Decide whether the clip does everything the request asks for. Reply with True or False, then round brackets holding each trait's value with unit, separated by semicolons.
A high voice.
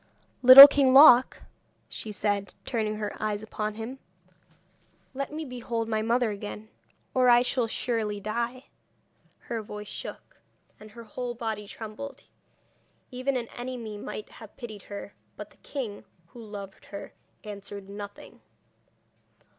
True (225 Hz)